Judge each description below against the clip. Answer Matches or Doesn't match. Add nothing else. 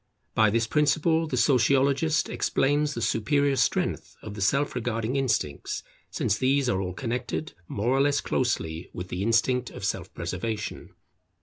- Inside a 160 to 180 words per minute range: Doesn't match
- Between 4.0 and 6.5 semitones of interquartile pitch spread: Matches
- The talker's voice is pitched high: Doesn't match